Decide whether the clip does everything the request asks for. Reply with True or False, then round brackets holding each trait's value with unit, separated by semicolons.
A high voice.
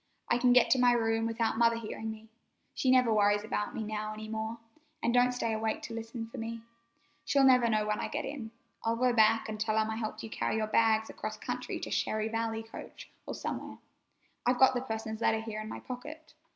True (225 Hz)